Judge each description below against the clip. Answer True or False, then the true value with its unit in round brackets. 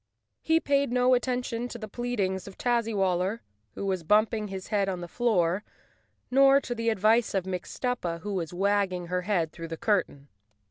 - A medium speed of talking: True (185 wpm)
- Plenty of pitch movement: False (4.8 semitones)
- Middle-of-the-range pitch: False (205 Hz)